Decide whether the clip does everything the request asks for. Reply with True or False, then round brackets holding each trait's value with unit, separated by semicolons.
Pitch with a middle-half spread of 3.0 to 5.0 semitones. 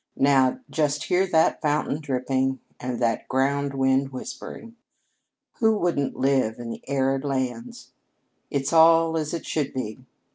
True (3.4 semitones)